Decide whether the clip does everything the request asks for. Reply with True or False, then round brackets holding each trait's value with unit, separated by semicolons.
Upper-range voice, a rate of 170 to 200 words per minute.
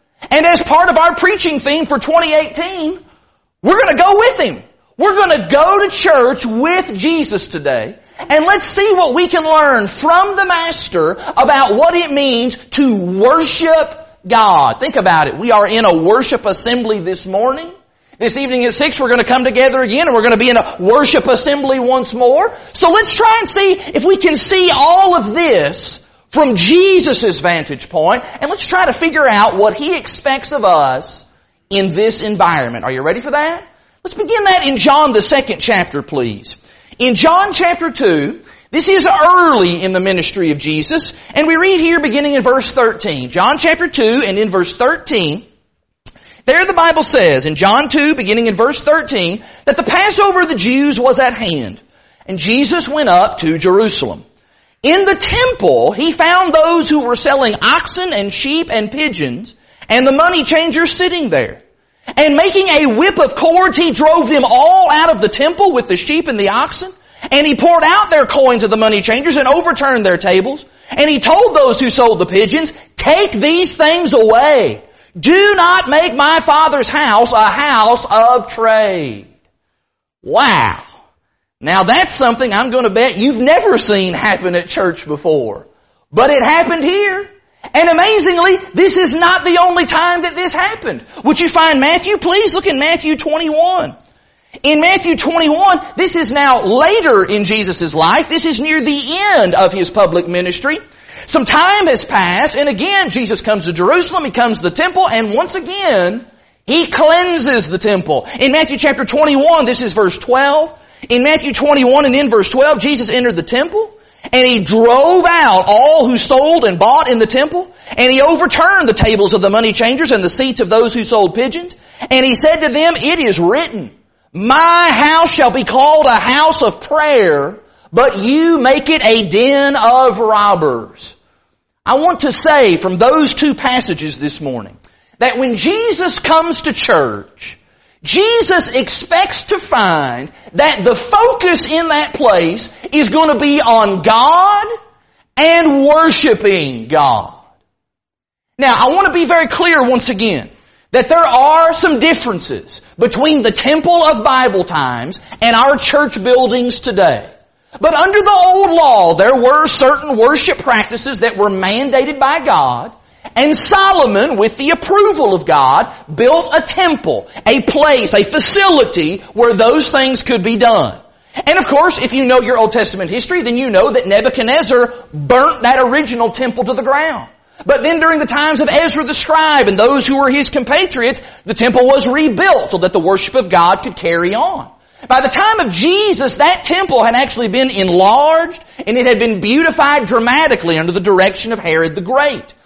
True (285 Hz; 175 wpm)